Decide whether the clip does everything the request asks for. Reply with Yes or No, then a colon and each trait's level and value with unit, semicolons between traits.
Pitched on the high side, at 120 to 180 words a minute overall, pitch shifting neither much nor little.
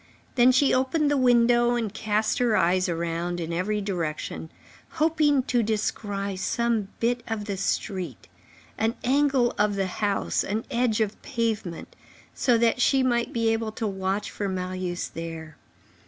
Yes: high, 220 Hz; average, 155 wpm; average, 4.2 semitones